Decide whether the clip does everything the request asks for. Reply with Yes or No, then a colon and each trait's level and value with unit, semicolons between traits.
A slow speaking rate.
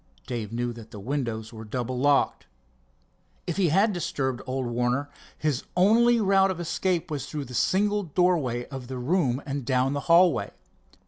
No: average, 170 wpm